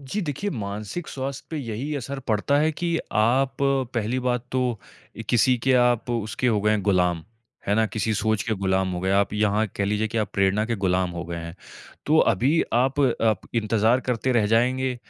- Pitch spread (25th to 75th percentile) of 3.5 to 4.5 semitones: Yes, average, 4.2 semitones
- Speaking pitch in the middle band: No, low, 115 Hz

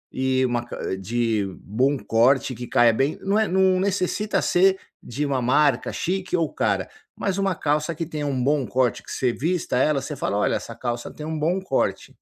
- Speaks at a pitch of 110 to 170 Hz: Yes, medium, 140 Hz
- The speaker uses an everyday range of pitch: No, wide, 6.7 semitones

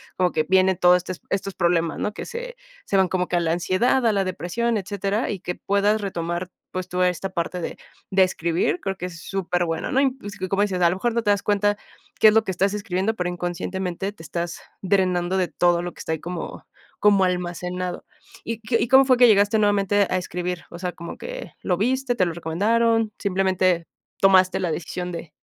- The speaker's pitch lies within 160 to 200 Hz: Yes, medium, 185 Hz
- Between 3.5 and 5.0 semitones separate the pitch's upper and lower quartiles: No, narrow, 2.6 semitones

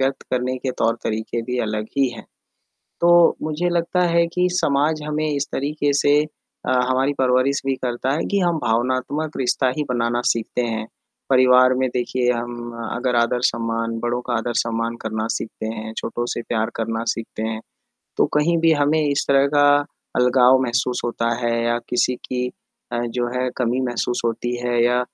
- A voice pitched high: No, low, 125 Hz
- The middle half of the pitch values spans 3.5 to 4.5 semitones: No, average, 3.0 semitones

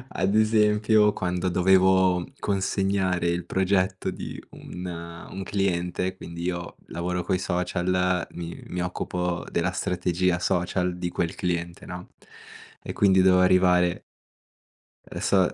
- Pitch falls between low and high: No, very low, 90 Hz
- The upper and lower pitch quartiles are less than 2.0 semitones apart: Yes, narrow, 1.2 semitones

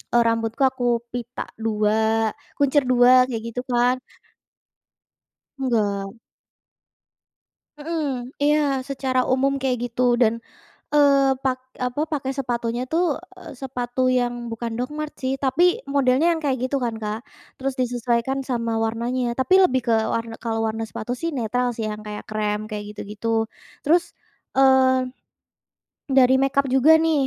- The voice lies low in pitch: No, very high, 250 Hz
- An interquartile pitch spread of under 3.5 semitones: Yes, average, 2.9 semitones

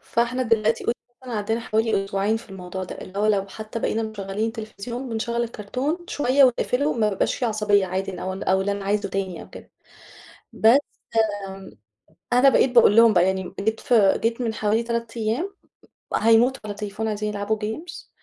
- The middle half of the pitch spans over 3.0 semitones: No, average, 2.7 semitones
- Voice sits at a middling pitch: No, high, 220 Hz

